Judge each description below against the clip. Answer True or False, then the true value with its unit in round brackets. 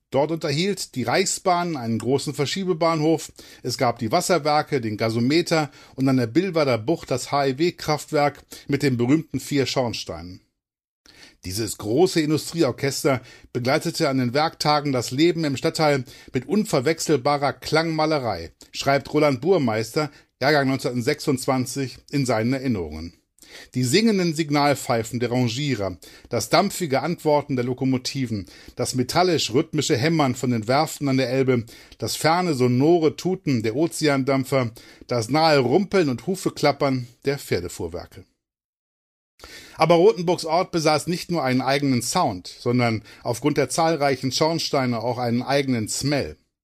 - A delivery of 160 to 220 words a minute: False (125 wpm)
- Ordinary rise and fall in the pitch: True (4.1 semitones)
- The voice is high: False (140 Hz)